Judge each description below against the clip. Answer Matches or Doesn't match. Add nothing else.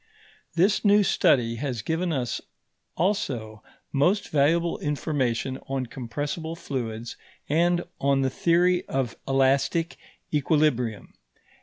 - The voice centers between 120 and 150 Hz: Matches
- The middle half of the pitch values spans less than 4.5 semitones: Doesn't match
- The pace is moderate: Doesn't match